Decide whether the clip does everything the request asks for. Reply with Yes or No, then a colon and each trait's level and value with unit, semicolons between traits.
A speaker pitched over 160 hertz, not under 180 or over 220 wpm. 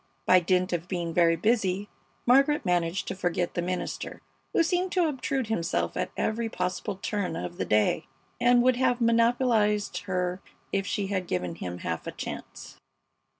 No: high, 190 Hz; average, 165 wpm